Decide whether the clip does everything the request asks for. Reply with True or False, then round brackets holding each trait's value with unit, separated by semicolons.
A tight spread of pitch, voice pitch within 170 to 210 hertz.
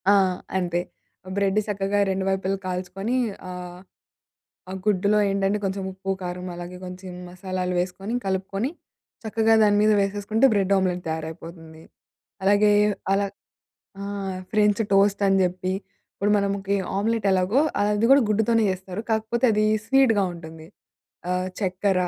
True (2.3 semitones; 195 Hz)